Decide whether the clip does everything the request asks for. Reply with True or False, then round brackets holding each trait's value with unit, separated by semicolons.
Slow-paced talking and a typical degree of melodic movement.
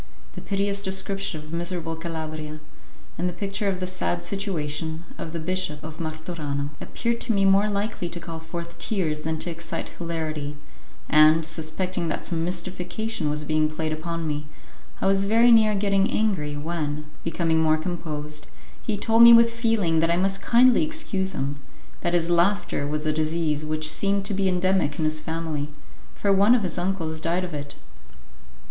False (175 wpm; 3.9 semitones)